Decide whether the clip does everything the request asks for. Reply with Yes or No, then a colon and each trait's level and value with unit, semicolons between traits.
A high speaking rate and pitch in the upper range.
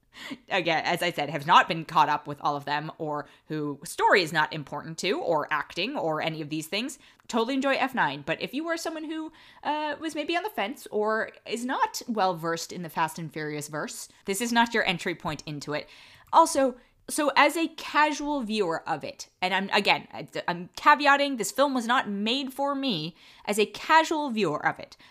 Yes: fast, 210 wpm; high, 210 Hz